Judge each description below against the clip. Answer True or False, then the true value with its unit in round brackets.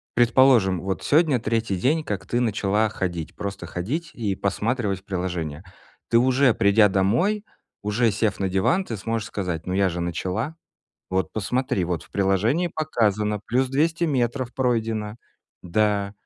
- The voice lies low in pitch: True (105 Hz)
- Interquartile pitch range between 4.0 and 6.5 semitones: True (4.7 semitones)